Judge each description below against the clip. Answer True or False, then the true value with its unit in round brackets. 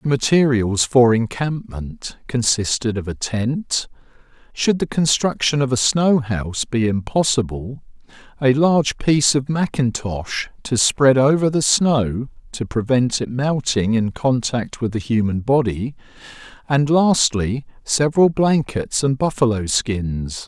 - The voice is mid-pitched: False (125 Hz)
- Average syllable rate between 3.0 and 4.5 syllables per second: True (4.0 syllables/s)